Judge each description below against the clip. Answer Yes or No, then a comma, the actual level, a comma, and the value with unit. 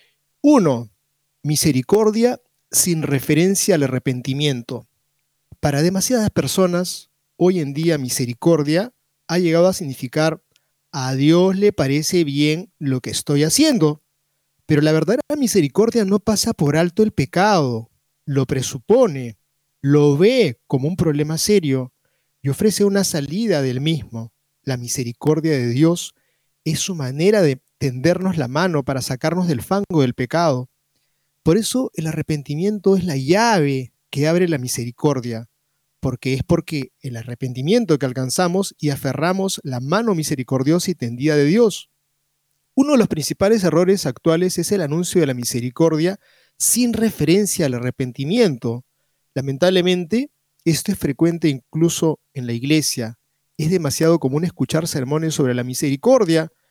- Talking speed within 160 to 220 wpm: No, average, 135 wpm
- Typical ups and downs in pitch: Yes, average, 4.9 semitones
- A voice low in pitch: No, medium, 155 Hz